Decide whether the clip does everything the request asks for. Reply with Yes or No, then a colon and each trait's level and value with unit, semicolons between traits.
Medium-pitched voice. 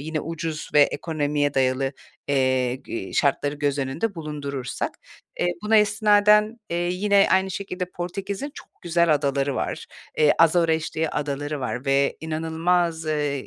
Yes: medium, 155 Hz